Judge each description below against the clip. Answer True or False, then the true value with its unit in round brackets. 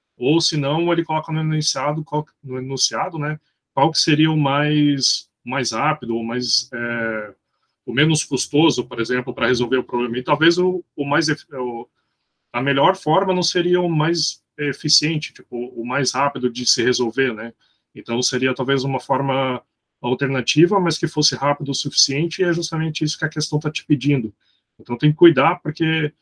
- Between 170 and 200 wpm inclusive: True (180 wpm)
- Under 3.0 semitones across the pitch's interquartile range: False (3.8 semitones)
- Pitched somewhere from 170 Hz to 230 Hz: False (145 Hz)